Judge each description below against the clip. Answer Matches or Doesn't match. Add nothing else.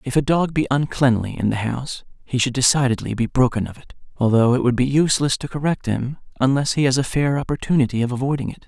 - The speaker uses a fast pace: Matches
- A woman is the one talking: Doesn't match